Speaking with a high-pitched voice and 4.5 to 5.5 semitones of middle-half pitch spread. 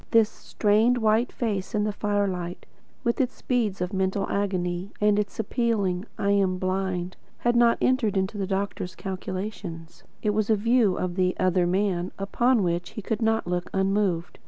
No: high, 200 Hz; average, 2.8 semitones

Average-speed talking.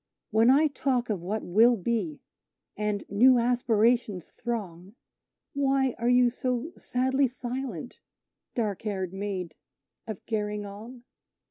No: slow, 120 wpm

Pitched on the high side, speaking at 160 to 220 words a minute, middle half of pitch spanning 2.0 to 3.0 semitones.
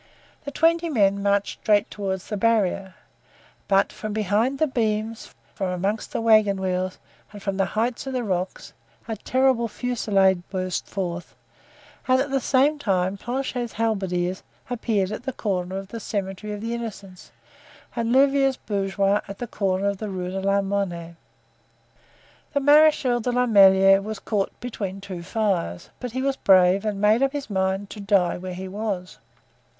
No: high, 205 Hz; average, 165 wpm; average, 3.7 semitones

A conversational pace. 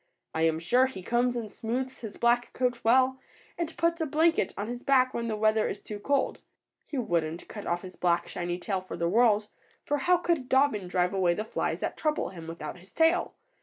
No: fast, 215 wpm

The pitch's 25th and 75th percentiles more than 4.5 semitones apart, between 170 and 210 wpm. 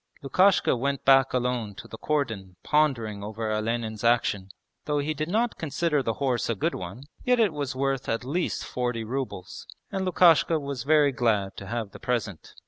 Yes: average, 4.9 semitones; average, 180 wpm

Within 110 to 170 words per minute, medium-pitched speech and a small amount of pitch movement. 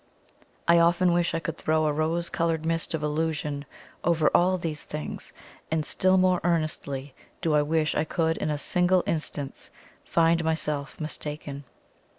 Yes: average, 160 wpm; medium, 160 Hz; narrow, 2.0 semitones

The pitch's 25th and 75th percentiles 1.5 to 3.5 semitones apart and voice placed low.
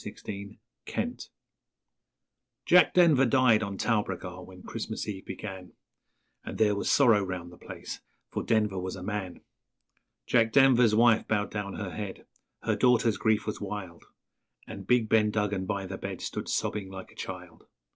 Yes: average, 2.9 semitones; low, 105 Hz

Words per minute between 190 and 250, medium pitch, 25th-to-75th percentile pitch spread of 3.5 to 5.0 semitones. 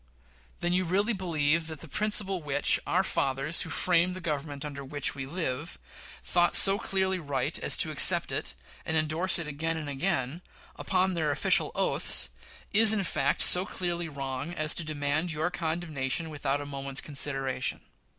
No: average, 170 wpm; medium, 160 Hz; average, 3.9 semitones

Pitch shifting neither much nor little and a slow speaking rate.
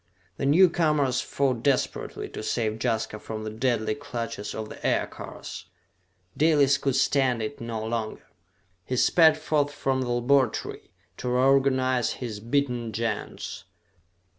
Yes: average, 3.7 semitones; slow, 130 wpm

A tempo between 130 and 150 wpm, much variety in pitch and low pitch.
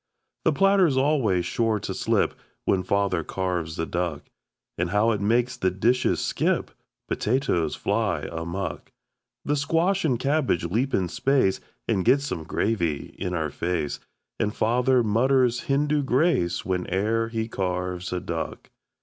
Yes: average, 140 wpm; wide, 6.6 semitones; low, 105 Hz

